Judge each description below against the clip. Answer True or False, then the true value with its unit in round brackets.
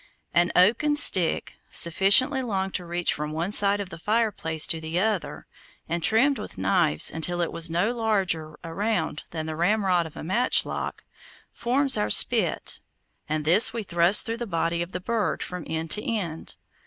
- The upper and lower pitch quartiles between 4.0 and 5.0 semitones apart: True (4.7 semitones)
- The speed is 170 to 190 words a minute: True (175 wpm)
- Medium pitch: True (180 Hz)